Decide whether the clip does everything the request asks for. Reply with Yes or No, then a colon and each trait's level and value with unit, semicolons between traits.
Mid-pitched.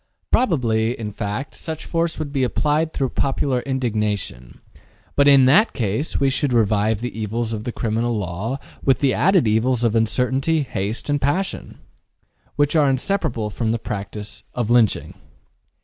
No: low, 120 Hz